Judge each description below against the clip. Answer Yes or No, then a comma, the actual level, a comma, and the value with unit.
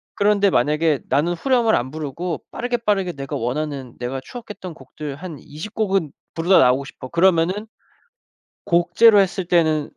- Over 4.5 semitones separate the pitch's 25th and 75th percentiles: Yes, wide, 5.4 semitones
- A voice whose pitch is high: No, medium, 165 Hz